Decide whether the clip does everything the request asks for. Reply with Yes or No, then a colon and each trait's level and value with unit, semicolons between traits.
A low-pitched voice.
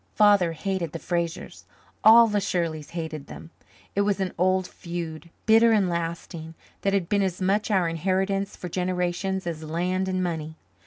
No: medium, 180 Hz